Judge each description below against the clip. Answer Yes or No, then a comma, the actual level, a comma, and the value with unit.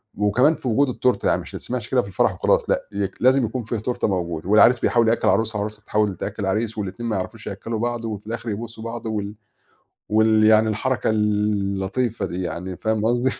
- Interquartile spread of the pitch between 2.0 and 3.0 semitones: Yes, narrow, 2.5 semitones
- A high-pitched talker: No, low, 110 Hz